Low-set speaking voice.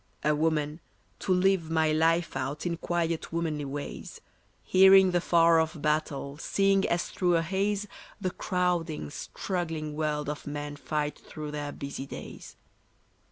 No: medium, 160 Hz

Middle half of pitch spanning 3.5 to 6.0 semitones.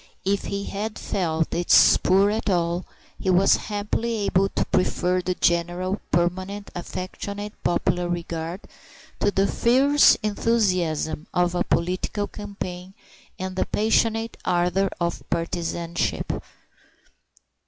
No: average, 2.7 semitones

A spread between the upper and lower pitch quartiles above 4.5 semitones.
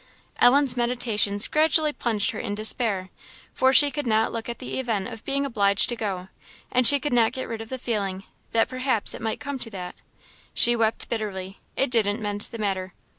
No: average, 3.8 semitones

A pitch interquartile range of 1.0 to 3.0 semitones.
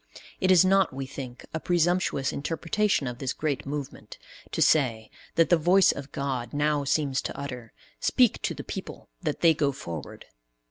No: average, 4.1 semitones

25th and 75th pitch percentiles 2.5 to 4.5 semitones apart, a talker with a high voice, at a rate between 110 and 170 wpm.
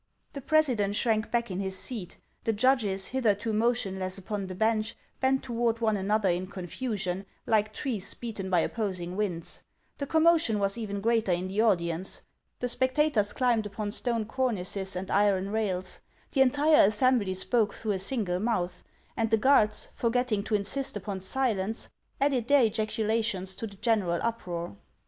Yes: average, 3.7 semitones; high, 215 Hz; average, 160 wpm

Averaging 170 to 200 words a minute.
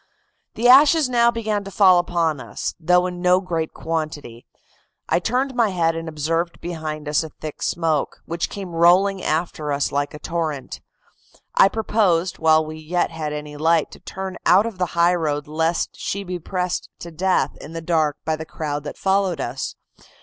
Yes: average, 185 wpm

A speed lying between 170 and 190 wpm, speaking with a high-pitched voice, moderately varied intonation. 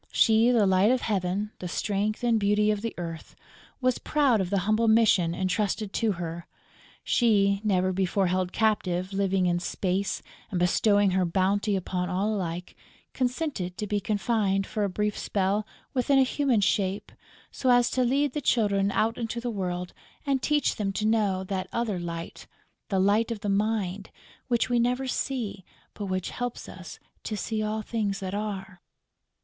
Yes: average, 175 wpm; high, 205 Hz; average, 3.3 semitones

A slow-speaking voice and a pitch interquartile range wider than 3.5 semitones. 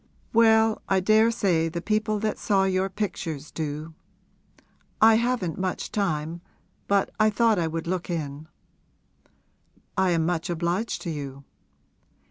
Yes: slow, 130 wpm; average, 4.8 semitones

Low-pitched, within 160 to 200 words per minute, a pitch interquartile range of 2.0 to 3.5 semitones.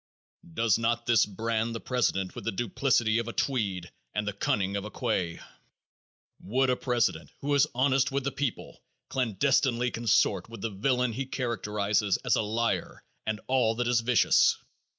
Yes: low, 115 Hz; average, 170 wpm; average, 3.2 semitones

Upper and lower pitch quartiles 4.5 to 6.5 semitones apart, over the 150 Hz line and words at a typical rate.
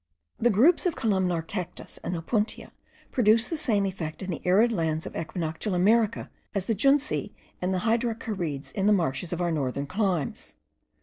Yes: average, 5.1 semitones; high, 190 Hz; average, 170 wpm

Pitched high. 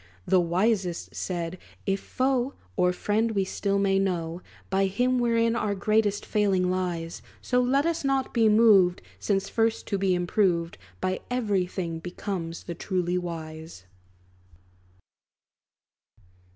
Yes: high, 195 Hz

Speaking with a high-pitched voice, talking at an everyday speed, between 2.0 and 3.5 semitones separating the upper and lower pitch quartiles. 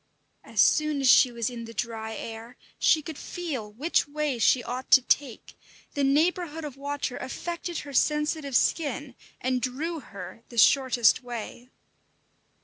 No: very high, 265 Hz; average, 150 wpm; average, 4.0 semitones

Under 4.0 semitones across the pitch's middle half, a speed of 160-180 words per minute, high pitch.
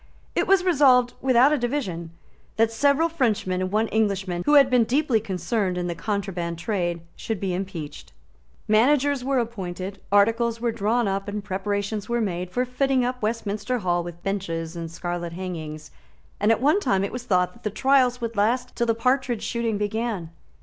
No: average, 5.0 semitones; average, 175 wpm; high, 215 Hz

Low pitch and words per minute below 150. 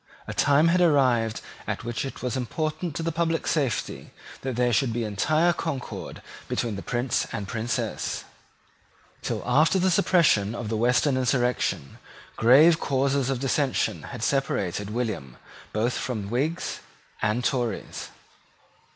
Yes: low, 125 Hz; average, 140 wpm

